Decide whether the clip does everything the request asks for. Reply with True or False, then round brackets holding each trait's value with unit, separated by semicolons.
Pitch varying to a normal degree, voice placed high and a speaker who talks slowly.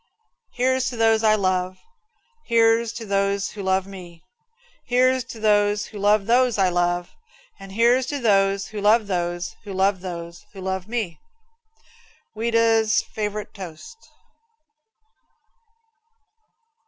True (3.3 semitones; 205 Hz; 125 wpm)